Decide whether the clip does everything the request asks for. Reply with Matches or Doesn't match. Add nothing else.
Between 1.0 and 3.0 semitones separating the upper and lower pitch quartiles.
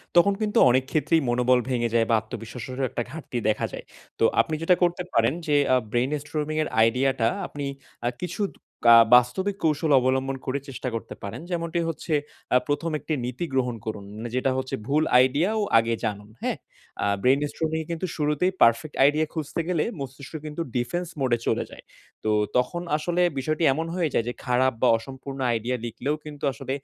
Doesn't match